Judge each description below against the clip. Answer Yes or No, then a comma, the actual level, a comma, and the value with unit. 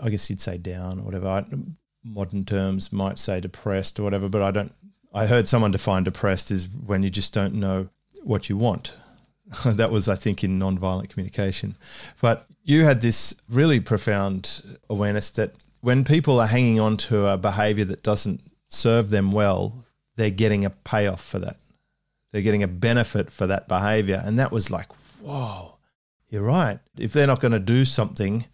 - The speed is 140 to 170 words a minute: No, average, 185 wpm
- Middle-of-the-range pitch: No, low, 105 Hz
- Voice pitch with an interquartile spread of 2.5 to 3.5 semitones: Yes, average, 3.2 semitones